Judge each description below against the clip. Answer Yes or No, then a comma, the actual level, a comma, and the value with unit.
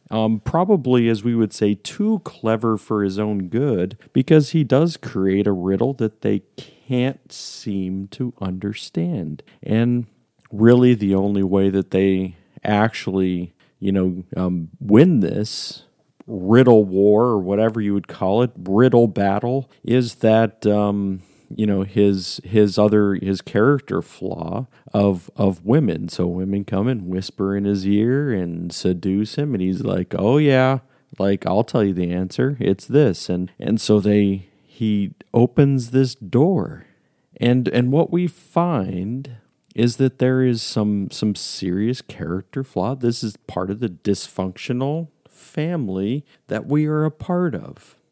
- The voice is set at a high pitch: No, low, 105 Hz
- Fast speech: No, average, 150 wpm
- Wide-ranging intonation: No, average, 4.8 semitones